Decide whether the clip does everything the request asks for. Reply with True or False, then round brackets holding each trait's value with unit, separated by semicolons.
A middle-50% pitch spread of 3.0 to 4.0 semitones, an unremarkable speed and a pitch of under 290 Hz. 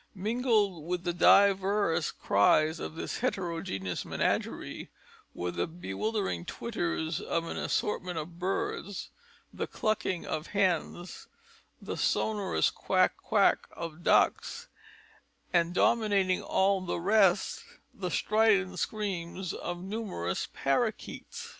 False (3.6 semitones; 110 wpm; 185 Hz)